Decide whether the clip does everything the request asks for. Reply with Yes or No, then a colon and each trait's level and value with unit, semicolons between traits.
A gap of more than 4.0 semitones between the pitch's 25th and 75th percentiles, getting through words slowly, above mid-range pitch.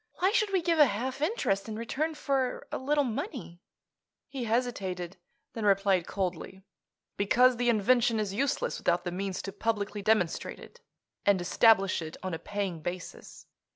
No: average, 5.1 semitones; average, 160 wpm; high, 215 Hz